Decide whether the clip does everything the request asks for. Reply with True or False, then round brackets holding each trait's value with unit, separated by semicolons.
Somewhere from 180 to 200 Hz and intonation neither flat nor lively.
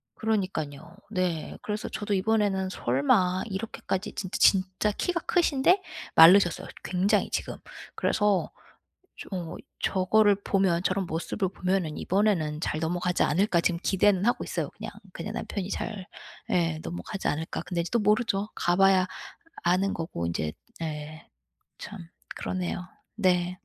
True (185 Hz; 3.1 semitones)